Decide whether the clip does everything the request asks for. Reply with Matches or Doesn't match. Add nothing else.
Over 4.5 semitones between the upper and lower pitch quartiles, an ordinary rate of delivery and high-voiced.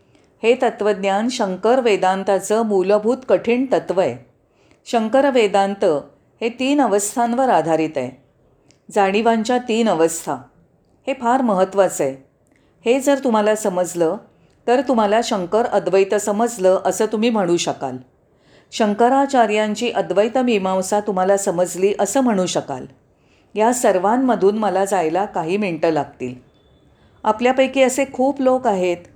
Doesn't match